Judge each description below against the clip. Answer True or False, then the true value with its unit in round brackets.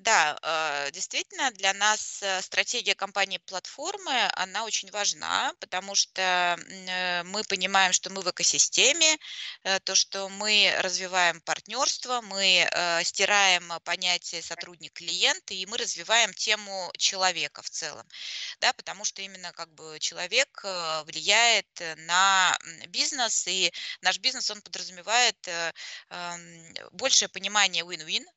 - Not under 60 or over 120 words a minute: True (110 wpm)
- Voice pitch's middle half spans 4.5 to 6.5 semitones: False (3.3 semitones)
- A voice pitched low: False (190 Hz)